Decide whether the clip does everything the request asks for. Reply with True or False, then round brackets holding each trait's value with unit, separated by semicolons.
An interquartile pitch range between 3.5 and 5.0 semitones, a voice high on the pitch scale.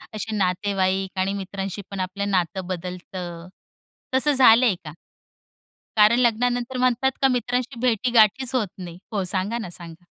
True (4.7 semitones; 200 Hz)